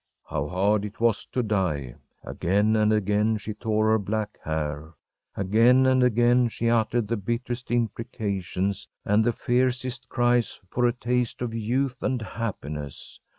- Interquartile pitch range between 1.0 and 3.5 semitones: Yes, average, 3.2 semitones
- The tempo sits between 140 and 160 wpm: Yes, average, 150 wpm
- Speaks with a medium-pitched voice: No, low, 110 Hz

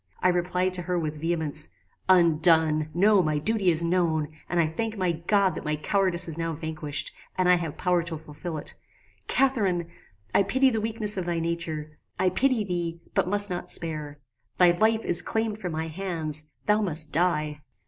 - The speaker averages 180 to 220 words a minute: Yes, average, 185 wpm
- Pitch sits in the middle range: Yes, medium, 175 Hz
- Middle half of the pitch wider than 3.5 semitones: No, average, 3.2 semitones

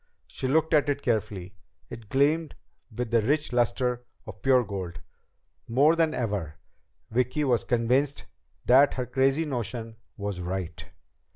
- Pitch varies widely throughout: No, average, 4.4 semitones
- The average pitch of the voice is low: Yes, low, 125 Hz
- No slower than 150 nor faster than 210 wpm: No, slow, 135 wpm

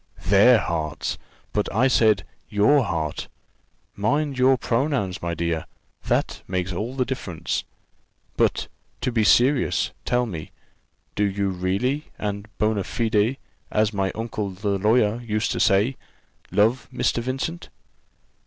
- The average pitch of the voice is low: Yes, low, 105 Hz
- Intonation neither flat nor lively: Yes, average, 4.3 semitones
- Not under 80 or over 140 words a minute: Yes, slow, 135 wpm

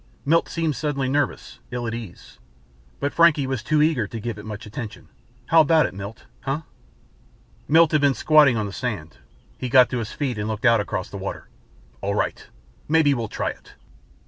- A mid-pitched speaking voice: No, low, 125 Hz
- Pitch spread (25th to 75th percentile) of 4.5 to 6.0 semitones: Yes, wide, 5.4 semitones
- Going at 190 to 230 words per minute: Yes, average, 195 wpm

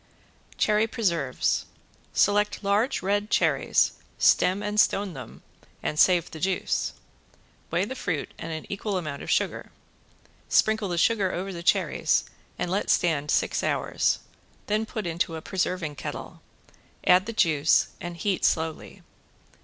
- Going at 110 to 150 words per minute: Yes, average, 140 wpm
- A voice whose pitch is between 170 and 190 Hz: Yes, medium, 185 Hz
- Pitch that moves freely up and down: No, average, 3.9 semitones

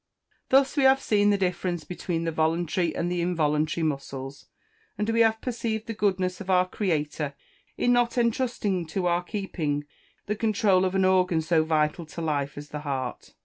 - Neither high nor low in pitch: Yes, medium, 180 Hz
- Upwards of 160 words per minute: Yes, average, 185 wpm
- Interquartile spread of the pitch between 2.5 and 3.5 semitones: No, average, 4.8 semitones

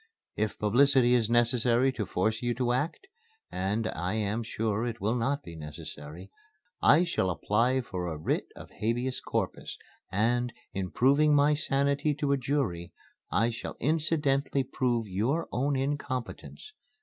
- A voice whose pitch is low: Yes, low, 120 Hz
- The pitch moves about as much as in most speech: Yes, average, 4.7 semitones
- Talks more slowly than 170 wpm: Yes, average, 150 wpm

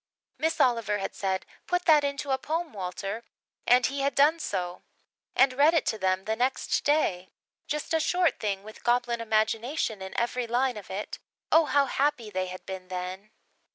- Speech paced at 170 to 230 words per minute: Yes, average, 185 wpm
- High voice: Yes, high, 240 Hz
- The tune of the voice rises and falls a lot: Yes, wide, 6.4 semitones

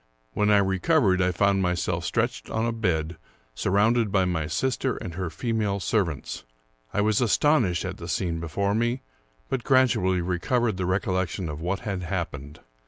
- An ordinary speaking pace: Yes, average, 165 wpm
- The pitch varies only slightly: No, average, 4.1 semitones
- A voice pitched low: Yes, very low, 95 Hz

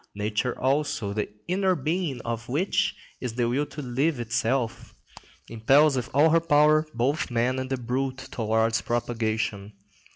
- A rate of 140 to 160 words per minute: Yes, average, 150 wpm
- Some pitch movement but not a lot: Yes, average, 4.2 semitones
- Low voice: Yes, low, 125 Hz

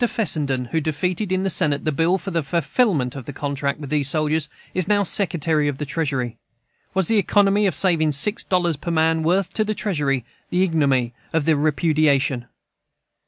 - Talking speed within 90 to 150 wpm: No, average, 185 wpm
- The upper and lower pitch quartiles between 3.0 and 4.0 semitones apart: No, average, 4.4 semitones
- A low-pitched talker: No, medium, 160 Hz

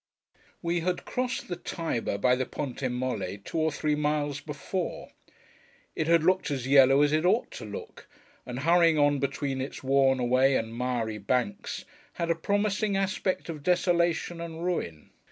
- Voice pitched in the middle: Yes, medium, 145 Hz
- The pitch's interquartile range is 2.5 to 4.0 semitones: No, average, 4.8 semitones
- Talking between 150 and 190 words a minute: Yes, average, 165 wpm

